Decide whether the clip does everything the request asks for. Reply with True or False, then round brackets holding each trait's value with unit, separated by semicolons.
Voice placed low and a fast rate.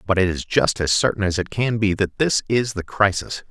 True (100 Hz; 255 wpm)